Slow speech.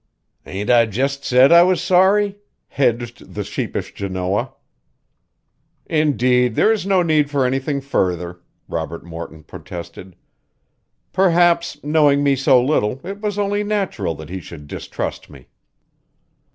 Yes: slow, 130 wpm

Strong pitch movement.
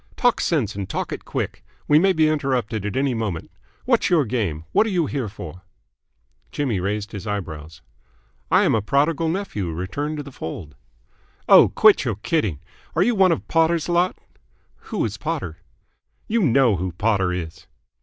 Yes: wide, 9.0 semitones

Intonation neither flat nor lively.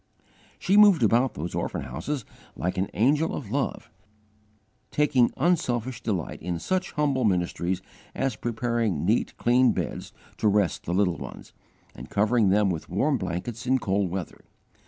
No: wide, 5.8 semitones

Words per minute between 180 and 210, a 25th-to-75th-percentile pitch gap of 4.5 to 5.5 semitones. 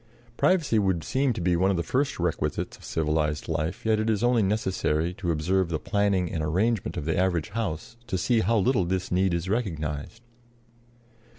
Yes: average, 190 wpm; average, 5.0 semitones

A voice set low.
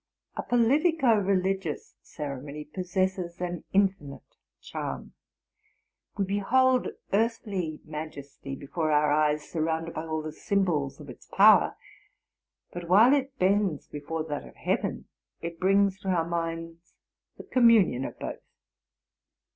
No: medium, 175 Hz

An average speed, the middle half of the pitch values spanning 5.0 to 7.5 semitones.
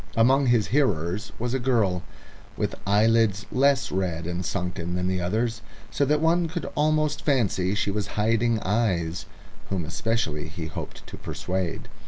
Yes: average, 155 wpm; wide, 5.4 semitones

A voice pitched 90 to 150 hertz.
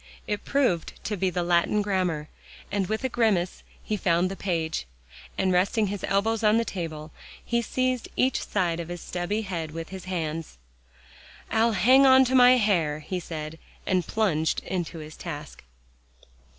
No: medium, 185 Hz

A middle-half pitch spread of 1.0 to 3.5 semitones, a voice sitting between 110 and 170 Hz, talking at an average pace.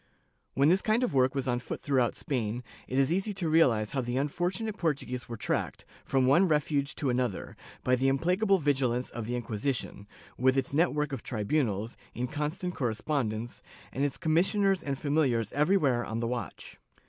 No: average, 4.5 semitones; low, 135 Hz; average, 185 wpm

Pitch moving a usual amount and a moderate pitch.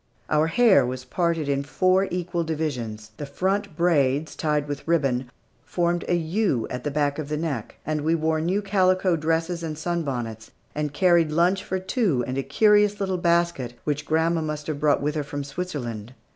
Yes: average, 3.7 semitones; medium, 155 Hz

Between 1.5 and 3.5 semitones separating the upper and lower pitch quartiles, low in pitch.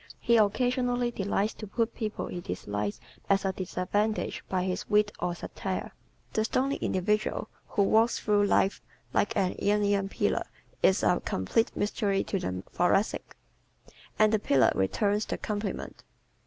No: narrow, 2.6 semitones; high, 205 Hz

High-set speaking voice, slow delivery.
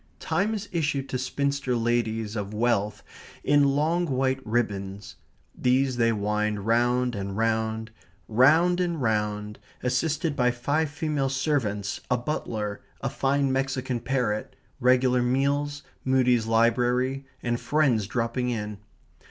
No: low, 125 Hz; slow, 125 wpm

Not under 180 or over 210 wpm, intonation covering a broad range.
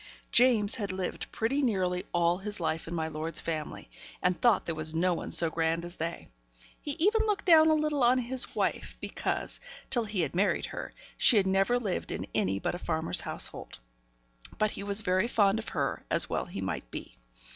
Yes: average, 200 wpm; wide, 6.2 semitones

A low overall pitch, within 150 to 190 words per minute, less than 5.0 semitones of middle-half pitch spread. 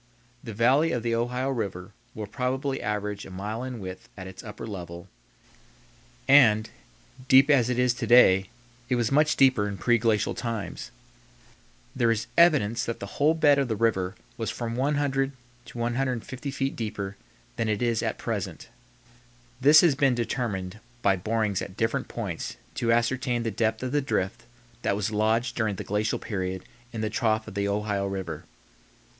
Yes: low, 115 Hz; average, 170 wpm; average, 3.9 semitones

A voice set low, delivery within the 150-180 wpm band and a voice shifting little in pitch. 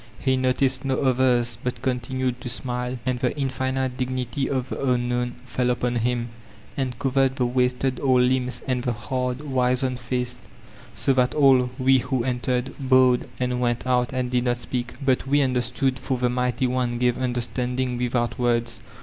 Yes: low, 125 Hz; average, 175 wpm; narrow, 1.0 semitones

